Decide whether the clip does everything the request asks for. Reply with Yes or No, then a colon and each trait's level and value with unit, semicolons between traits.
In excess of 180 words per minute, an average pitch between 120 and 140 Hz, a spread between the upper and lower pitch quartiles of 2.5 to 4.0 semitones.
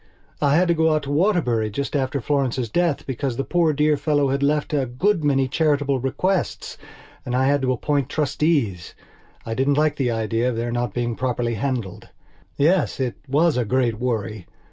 Yes: average, 190 wpm; low, 135 Hz; average, 3.7 semitones